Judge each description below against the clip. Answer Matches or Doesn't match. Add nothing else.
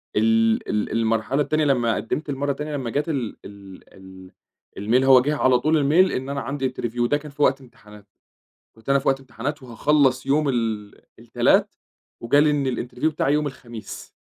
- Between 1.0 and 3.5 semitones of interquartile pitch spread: Doesn't match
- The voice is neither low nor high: Doesn't match